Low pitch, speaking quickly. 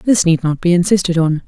No: medium, 175 Hz; fast, 245 wpm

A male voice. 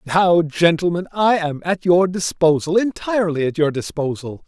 Yes: male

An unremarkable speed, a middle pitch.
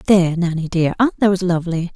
Yes: average, 185 wpm; medium, 180 Hz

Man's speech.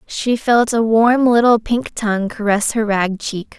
No: female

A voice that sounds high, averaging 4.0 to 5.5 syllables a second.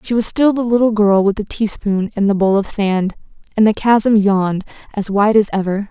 Yes: high, 205 Hz; 5.1 syllables/s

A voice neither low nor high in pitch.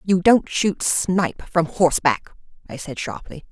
Yes: medium, 170 Hz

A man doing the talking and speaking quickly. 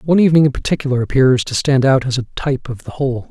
Yes: male; fast, 255 wpm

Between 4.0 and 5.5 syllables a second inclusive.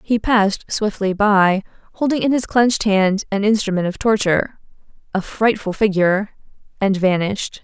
Yes: 5.1 syllables/s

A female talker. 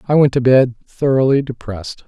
No: male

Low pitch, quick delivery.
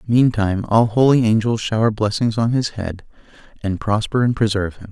No: low, 110 Hz; average, 170 wpm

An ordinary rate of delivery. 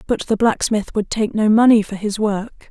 No: fast, 220 wpm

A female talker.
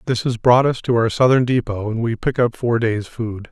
No: male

